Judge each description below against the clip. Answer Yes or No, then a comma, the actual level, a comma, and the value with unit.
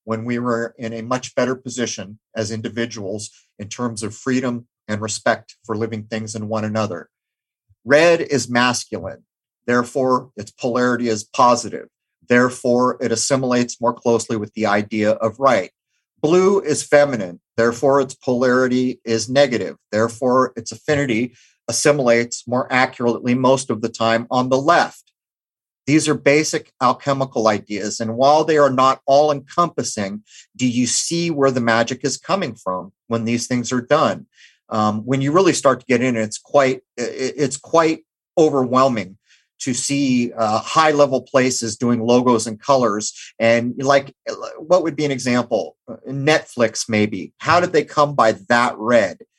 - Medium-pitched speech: No, low, 125 Hz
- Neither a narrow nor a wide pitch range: Yes, average, 3.1 semitones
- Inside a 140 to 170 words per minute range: Yes, average, 155 wpm